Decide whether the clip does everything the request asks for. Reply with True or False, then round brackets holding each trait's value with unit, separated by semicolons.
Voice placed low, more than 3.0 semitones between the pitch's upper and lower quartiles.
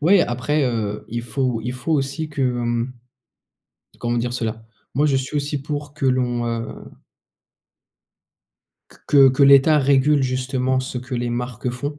False (130 Hz; 2.7 semitones)